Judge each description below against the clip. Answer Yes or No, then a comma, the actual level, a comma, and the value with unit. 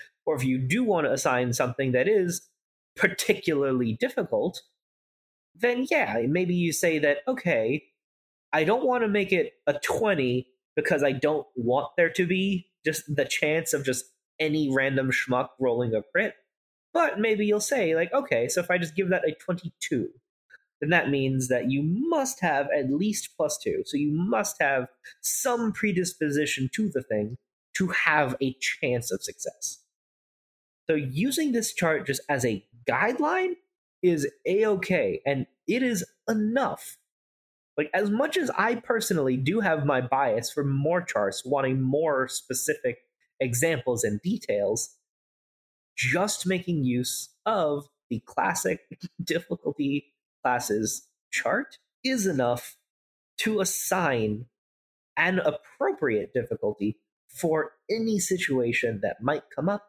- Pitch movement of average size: No, wide, 8.1 semitones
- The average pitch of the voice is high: No, medium, 155 Hz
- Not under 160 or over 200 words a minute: No, average, 140 wpm